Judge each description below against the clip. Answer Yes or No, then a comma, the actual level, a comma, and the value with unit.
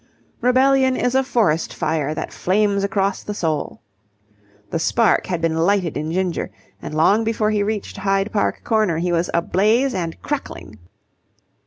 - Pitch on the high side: Yes, high, 195 Hz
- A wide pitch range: No, average, 4.8 semitones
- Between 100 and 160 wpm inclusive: Yes, average, 155 wpm